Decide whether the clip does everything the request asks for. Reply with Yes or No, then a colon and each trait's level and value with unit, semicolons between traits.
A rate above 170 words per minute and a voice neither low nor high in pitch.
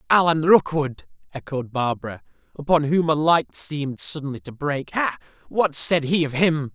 No: average, 160 wpm; medium, 145 Hz